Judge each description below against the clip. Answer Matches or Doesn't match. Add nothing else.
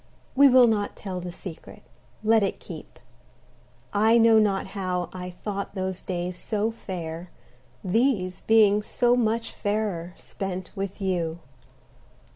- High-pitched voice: Matches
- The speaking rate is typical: Doesn't match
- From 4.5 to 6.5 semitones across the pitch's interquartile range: Doesn't match